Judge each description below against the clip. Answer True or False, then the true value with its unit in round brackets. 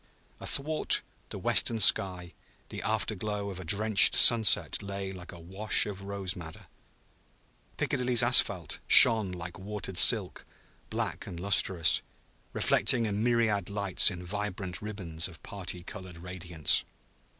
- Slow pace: True (130 wpm)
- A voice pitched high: False (95 Hz)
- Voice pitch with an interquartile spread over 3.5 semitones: False (2.9 semitones)